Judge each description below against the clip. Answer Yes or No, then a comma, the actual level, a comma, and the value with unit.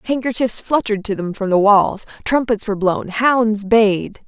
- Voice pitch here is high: Yes, high, 215 Hz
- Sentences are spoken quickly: No, average, 170 wpm